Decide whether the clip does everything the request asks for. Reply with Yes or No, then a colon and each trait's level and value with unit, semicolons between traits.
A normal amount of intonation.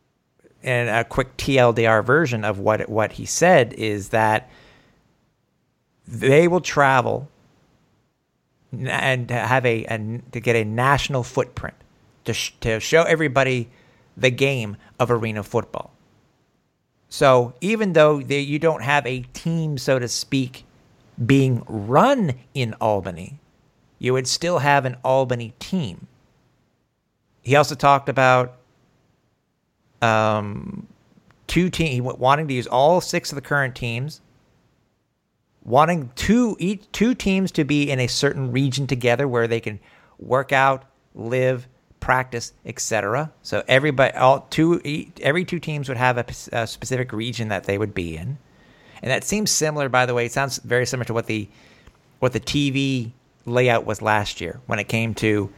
Yes: average, 3.4 semitones